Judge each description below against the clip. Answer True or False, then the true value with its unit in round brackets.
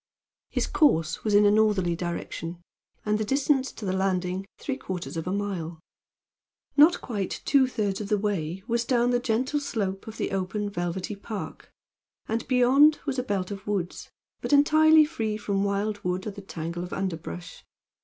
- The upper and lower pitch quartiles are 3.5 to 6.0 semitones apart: True (4.7 semitones)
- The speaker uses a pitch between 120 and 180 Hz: False (205 Hz)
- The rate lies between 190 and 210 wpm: False (175 wpm)